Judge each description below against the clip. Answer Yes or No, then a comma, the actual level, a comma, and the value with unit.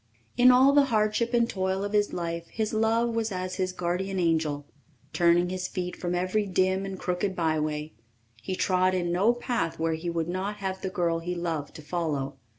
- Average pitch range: Yes, average, 3.4 semitones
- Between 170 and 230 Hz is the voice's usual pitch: Yes, medium, 185 Hz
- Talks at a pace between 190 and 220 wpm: Yes, average, 195 wpm